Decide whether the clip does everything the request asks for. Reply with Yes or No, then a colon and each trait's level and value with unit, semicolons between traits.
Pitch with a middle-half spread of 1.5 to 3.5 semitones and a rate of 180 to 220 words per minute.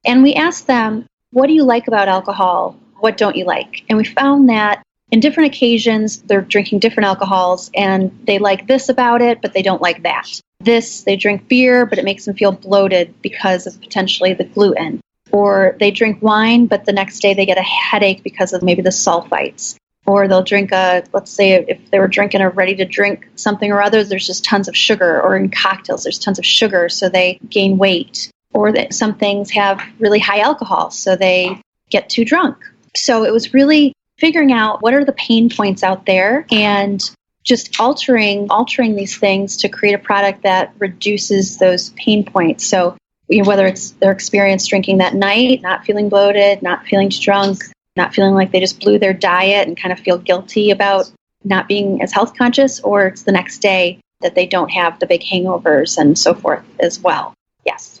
Yes: average, 2.8 semitones; average, 200 wpm